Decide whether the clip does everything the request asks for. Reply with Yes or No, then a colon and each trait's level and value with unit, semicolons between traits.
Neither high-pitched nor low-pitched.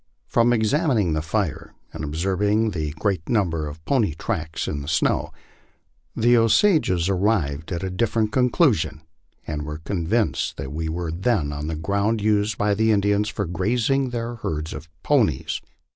No: low, 100 Hz